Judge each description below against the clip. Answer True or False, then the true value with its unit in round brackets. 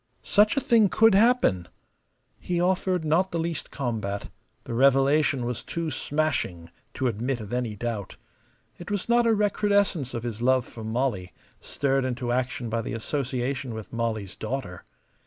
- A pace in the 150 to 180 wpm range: True (155 wpm)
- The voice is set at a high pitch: False (130 Hz)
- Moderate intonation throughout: False (6.7 semitones)